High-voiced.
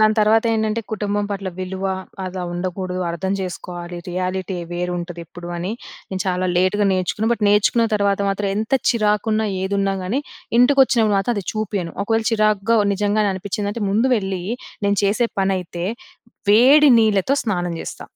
Yes: high, 200 Hz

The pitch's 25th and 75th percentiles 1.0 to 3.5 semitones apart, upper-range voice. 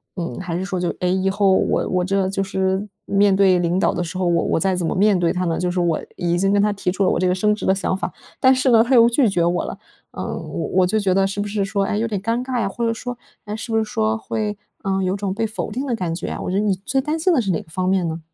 Yes: average, 2.8 semitones; high, 195 Hz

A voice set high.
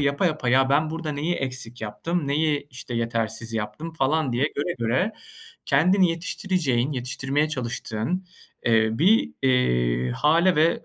No: medium, 140 Hz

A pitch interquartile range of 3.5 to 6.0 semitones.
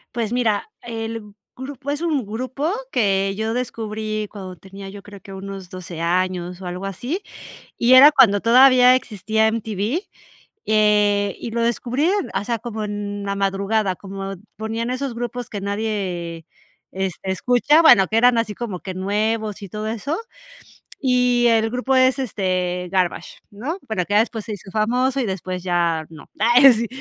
Yes: average, 3.8 semitones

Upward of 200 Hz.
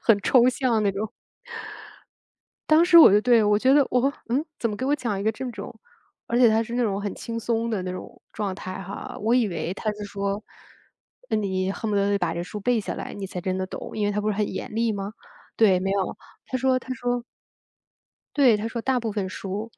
Yes: high, 215 Hz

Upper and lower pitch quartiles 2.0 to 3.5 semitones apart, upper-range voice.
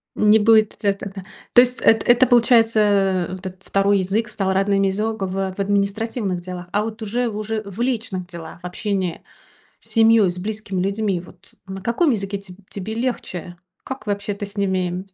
Yes: average, 2.7 semitones; high, 200 Hz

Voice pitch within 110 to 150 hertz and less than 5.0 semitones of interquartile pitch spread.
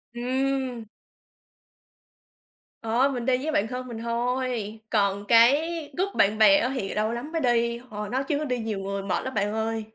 No: high, 235 Hz; average, 3.2 semitones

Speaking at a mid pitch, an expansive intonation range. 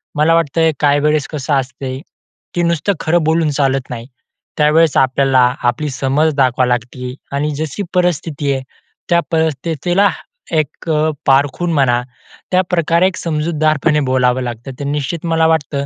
No: medium, 150 Hz; average, 3.4 semitones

